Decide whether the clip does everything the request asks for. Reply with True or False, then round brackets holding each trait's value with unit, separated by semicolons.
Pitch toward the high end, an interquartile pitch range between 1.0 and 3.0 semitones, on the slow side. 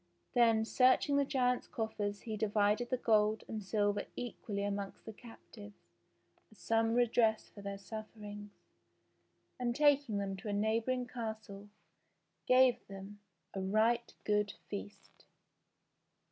True (220 Hz; 2.7 semitones; 125 wpm)